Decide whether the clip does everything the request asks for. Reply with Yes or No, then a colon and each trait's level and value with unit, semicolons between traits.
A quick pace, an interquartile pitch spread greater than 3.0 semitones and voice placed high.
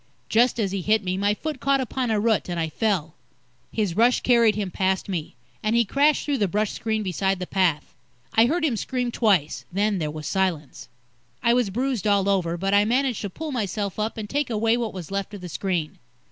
Yes: fast, 220 wpm; average, 3.9 semitones; high, 210 Hz